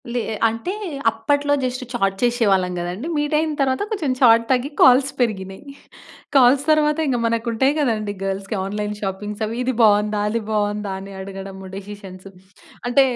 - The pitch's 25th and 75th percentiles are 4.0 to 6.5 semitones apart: Yes, average, 4.7 semitones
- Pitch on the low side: No, high, 225 Hz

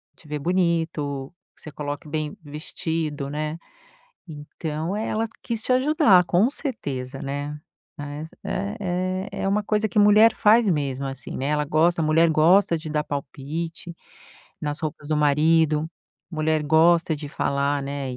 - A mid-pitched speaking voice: Yes, medium, 155 Hz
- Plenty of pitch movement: No, average, 3.3 semitones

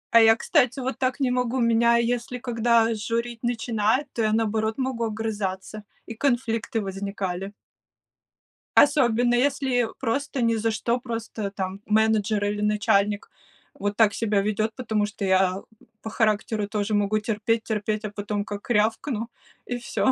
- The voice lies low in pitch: No, high, 225 Hz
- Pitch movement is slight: Yes, narrow, 2.3 semitones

